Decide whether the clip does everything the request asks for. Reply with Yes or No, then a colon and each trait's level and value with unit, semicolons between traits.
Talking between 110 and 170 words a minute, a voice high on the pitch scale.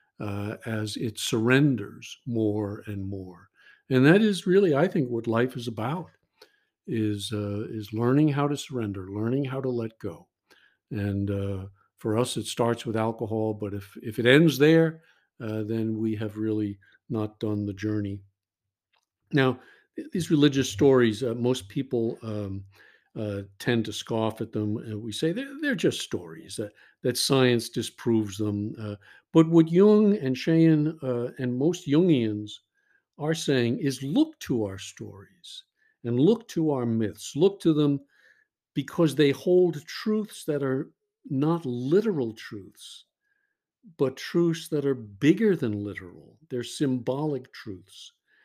No: average, 150 wpm; low, 125 Hz